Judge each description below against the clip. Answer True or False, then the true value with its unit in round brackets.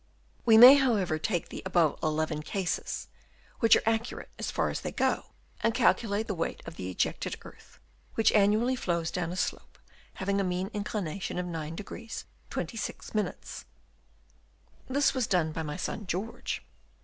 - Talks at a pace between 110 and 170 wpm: True (155 wpm)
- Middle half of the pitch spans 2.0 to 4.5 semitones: False (5.0 semitones)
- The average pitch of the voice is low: False (195 Hz)